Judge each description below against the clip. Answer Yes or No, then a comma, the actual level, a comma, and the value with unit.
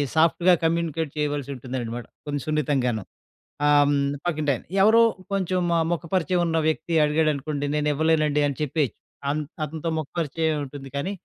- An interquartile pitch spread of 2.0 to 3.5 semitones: Yes, narrow, 2.4 semitones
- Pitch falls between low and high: Yes, medium, 150 Hz